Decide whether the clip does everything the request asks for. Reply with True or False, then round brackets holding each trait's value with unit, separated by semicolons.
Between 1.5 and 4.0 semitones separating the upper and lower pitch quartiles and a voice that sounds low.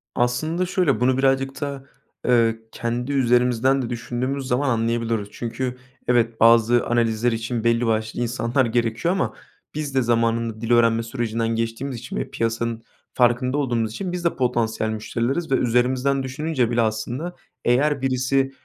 True (2.6 semitones; 120 Hz)